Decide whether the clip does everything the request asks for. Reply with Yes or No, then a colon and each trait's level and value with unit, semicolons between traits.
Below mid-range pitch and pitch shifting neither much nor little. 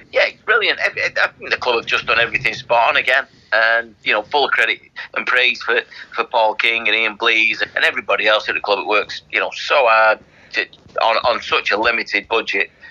No: low, 110 Hz; narrow, 1.1 semitones